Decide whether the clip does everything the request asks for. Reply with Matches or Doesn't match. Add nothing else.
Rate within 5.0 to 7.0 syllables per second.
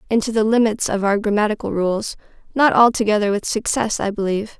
Matches